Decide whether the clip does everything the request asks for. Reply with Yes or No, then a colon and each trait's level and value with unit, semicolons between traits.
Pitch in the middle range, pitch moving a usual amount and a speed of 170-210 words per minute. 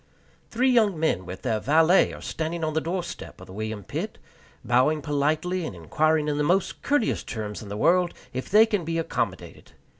No: medium, 155 Hz; wide, 6.2 semitones; average, 190 wpm